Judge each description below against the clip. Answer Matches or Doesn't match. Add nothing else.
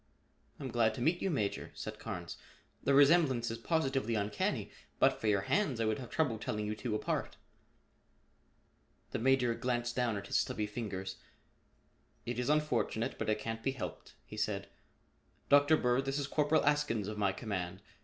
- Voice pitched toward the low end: Matches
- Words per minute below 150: Doesn't match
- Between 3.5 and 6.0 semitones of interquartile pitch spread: Matches